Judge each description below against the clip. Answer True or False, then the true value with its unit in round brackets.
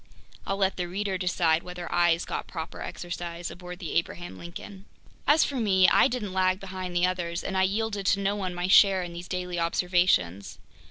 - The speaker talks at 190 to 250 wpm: True (195 wpm)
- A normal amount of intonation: False (1.8 semitones)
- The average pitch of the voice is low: False (180 Hz)